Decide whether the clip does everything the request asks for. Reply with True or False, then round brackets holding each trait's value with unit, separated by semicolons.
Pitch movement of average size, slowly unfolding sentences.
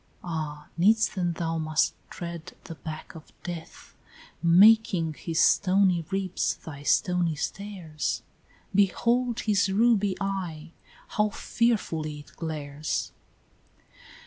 True (4.0 semitones; 105 wpm)